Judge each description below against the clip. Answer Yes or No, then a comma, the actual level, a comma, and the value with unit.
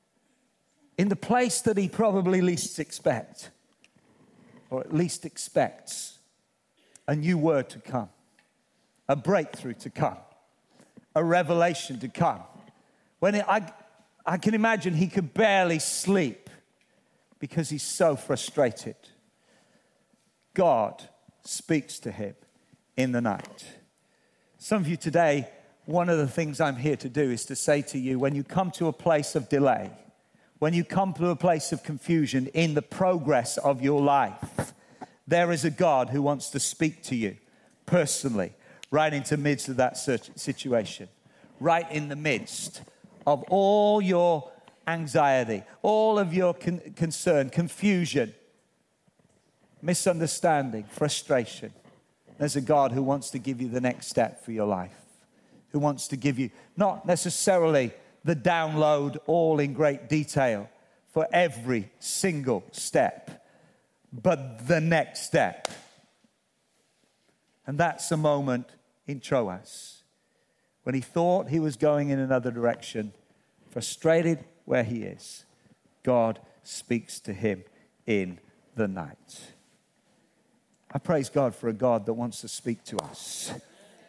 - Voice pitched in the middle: Yes, medium, 155 Hz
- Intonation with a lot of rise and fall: No, average, 4.5 semitones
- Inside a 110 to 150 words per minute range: Yes, slow, 135 wpm